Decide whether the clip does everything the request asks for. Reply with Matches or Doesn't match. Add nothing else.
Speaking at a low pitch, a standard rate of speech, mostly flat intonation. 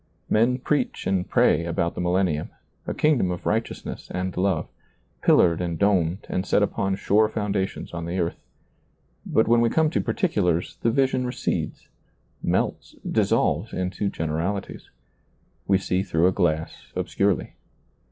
Doesn't match